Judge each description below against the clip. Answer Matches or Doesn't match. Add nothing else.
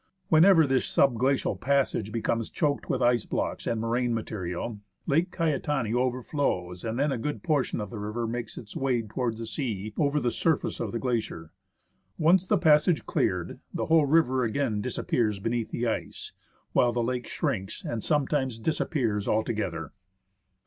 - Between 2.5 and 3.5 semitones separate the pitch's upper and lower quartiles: Doesn't match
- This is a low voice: Matches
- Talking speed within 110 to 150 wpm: Doesn't match